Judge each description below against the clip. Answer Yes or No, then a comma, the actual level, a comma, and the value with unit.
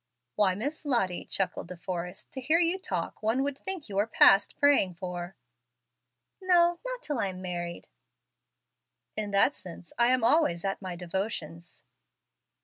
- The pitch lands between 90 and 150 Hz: No, high, 205 Hz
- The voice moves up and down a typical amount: No, wide, 8.0 semitones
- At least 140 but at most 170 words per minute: Yes, average, 155 wpm